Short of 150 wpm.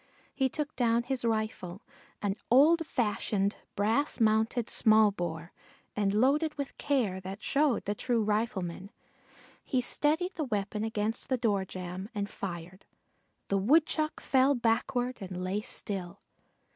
Yes: slow, 135 wpm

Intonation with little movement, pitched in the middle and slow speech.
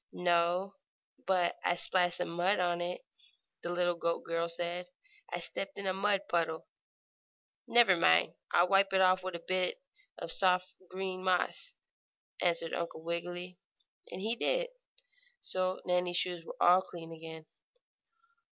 No: narrow, 1.6 semitones; medium, 180 Hz; average, 145 wpm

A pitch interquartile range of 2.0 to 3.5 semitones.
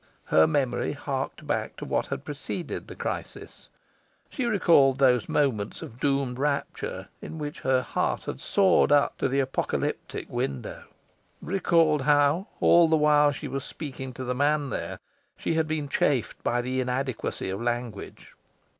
Yes: average, 2.8 semitones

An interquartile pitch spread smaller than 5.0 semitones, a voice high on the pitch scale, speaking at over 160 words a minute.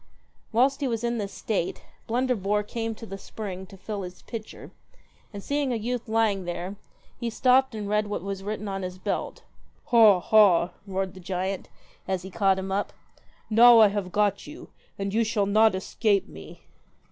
Yes: average, 2.9 semitones; high, 205 Hz; average, 190 wpm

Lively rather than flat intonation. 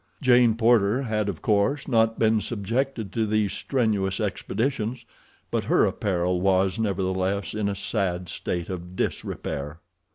No: average, 3.3 semitones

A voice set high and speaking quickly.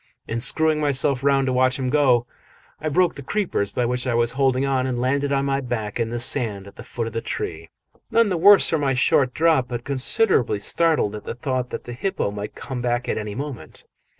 No: low, 130 Hz; fast, 230 wpm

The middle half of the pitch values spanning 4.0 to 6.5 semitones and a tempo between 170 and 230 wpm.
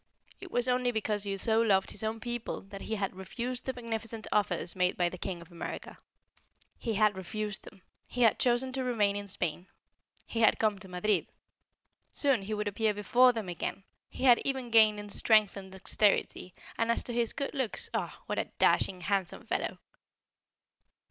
No: average, 3.5 semitones; average, 190 wpm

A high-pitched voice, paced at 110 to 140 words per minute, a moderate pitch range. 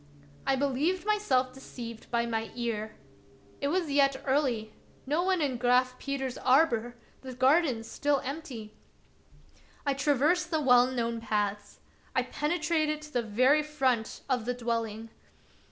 Yes: very high, 260 Hz; slow, 135 wpm; average, 4.0 semitones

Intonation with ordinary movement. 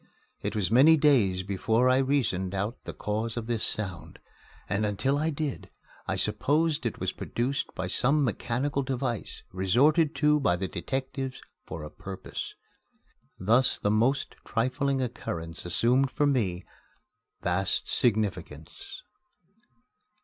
No: wide, 5.9 semitones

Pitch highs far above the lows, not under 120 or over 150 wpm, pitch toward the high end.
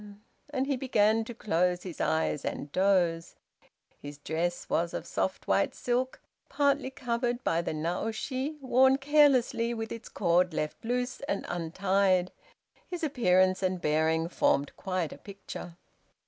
Yes: wide, 6.4 semitones; average, 140 wpm; high, 195 Hz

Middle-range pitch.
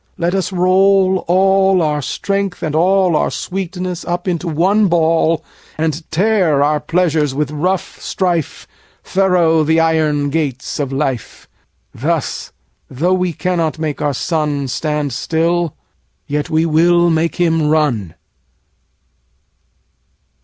Yes: medium, 165 Hz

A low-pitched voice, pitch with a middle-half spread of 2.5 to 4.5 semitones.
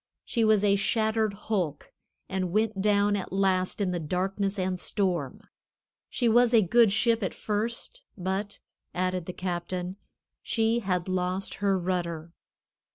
No: high, 195 Hz; average, 3.0 semitones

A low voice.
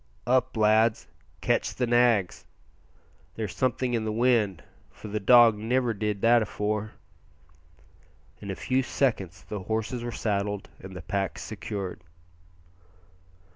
Yes: low, 110 Hz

